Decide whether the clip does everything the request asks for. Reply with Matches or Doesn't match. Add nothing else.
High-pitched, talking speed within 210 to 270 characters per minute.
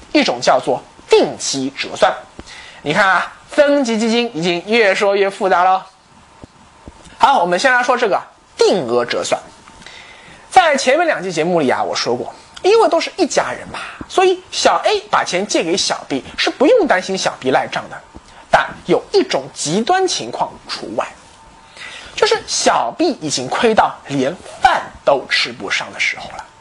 Matches